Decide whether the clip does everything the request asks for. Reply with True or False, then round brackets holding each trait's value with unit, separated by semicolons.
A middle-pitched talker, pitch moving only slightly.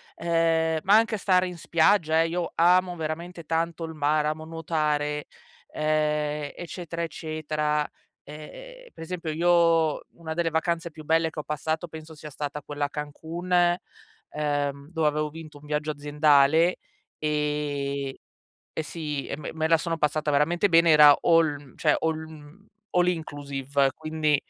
True (155 Hz; 2.0 semitones)